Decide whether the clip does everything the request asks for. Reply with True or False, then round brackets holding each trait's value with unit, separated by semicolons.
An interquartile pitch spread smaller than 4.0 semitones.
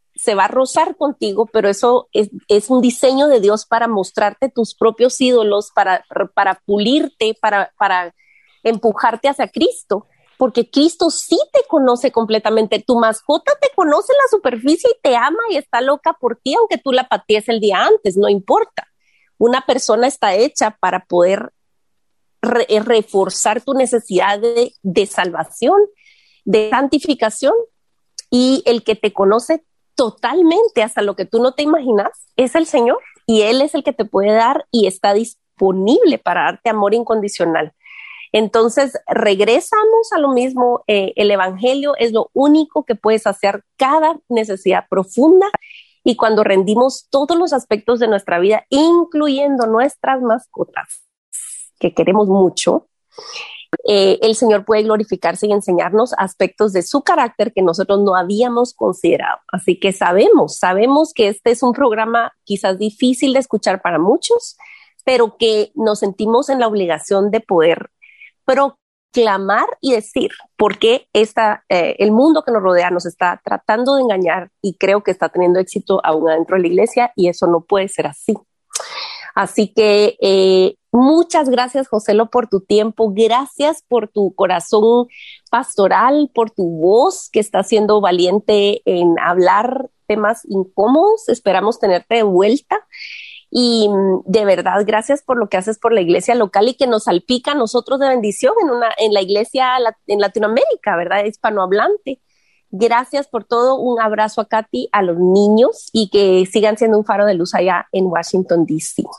False (4.7 semitones)